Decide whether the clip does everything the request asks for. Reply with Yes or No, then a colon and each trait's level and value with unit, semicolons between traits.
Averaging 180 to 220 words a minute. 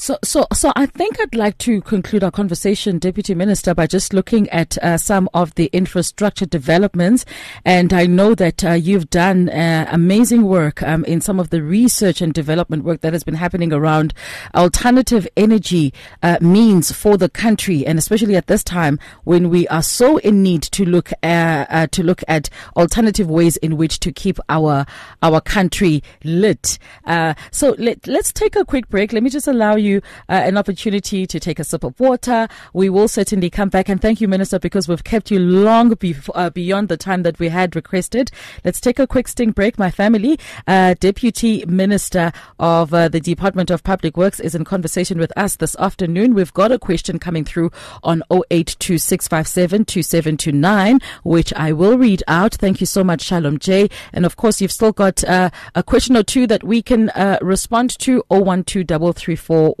Yes: average, 190 wpm